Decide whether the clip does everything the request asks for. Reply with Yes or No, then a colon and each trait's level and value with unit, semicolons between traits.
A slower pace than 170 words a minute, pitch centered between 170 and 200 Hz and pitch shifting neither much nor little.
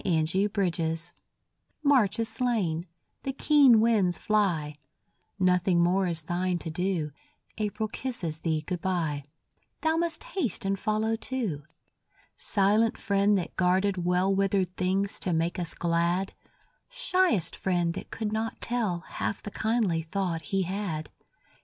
Yes: average, 145 wpm; high, 190 Hz; average, 4.1 semitones